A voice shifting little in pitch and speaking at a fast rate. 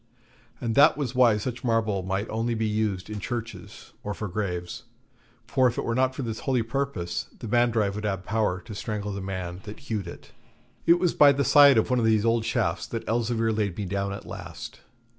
No: average, 3.2 semitones; fast, 215 wpm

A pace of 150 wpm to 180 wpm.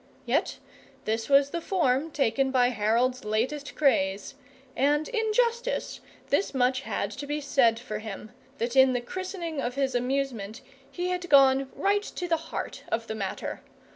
Yes: average, 165 wpm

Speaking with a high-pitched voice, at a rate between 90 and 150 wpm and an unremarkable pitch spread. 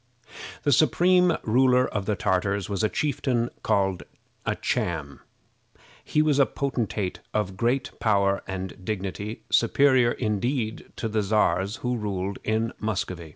No: low, 110 Hz; slow, 135 wpm; average, 4.5 semitones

